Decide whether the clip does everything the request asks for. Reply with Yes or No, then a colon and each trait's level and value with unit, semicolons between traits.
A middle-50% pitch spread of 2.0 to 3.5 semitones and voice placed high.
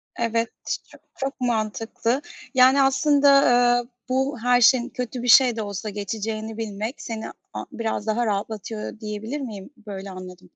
Yes: average, 3.0 semitones; high, 225 Hz